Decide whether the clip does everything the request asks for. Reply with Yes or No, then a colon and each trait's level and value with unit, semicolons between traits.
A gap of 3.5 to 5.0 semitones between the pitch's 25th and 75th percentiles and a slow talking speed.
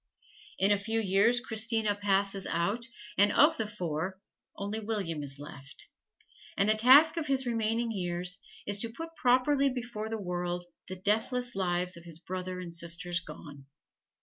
No: average, 4.5 semitones; average, 160 wpm